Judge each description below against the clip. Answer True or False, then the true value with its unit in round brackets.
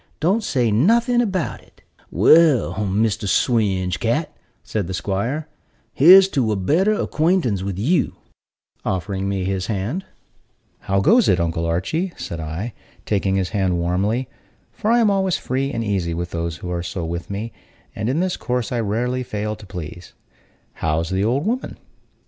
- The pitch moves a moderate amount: False (8.6 semitones)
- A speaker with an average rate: True (165 wpm)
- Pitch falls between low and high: False (105 Hz)